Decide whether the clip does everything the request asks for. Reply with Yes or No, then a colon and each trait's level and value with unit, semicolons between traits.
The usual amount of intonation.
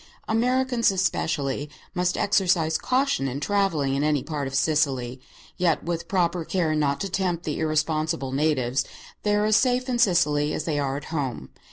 Yes: average, 5.0 semitones